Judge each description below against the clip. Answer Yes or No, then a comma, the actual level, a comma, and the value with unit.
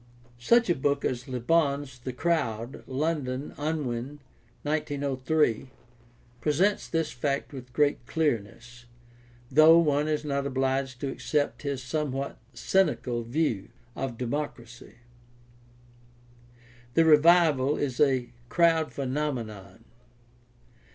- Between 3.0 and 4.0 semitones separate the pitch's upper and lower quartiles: Yes, average, 3.4 semitones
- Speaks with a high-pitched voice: No, medium, 140 Hz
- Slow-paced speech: Yes, slow, 105 wpm